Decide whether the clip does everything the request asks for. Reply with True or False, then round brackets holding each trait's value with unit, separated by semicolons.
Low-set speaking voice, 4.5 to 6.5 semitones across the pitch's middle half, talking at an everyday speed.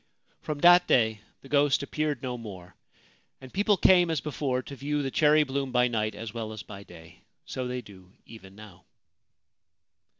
True (125 Hz; 5.4 semitones; 175 wpm)